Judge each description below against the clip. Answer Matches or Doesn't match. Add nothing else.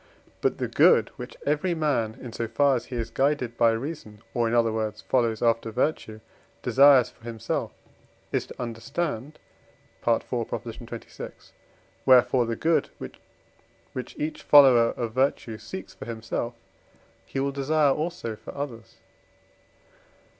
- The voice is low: Matches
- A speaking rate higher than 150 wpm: Doesn't match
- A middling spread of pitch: Matches